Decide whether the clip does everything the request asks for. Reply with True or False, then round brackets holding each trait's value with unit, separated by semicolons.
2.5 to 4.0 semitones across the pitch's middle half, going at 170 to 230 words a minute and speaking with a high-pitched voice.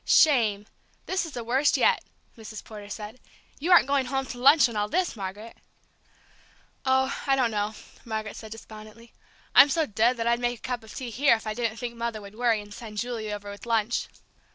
True (3.0 semitones; 205 wpm; 230 Hz)